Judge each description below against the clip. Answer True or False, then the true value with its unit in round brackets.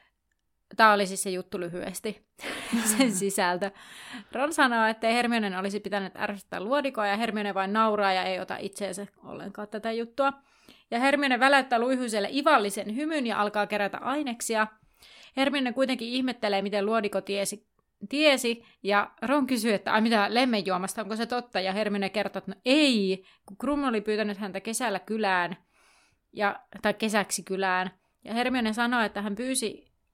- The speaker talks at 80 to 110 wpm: False (155 wpm)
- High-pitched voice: True (215 Hz)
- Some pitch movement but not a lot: True (3.5 semitones)